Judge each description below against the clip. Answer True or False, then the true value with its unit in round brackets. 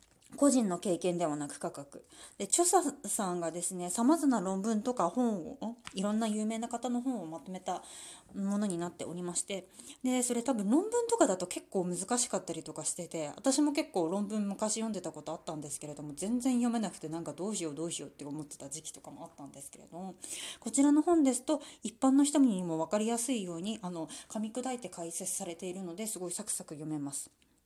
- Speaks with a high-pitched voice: True (200 Hz)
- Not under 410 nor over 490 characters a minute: True (415 characters per minute)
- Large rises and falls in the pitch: True (6.6 semitones)